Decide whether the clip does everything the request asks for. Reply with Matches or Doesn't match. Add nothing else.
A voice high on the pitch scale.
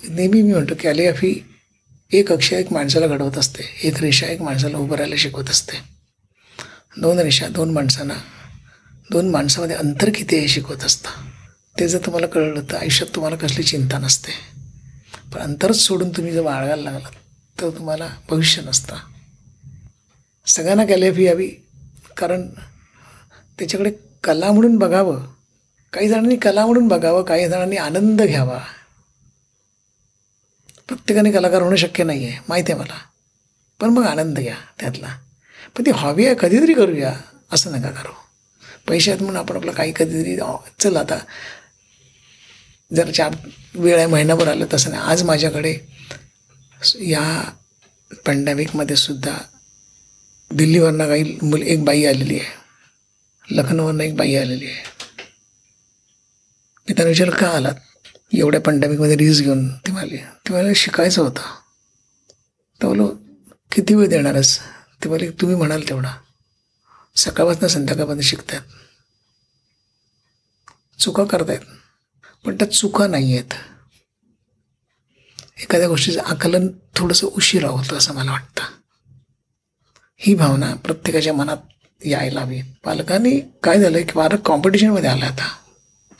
Doesn't match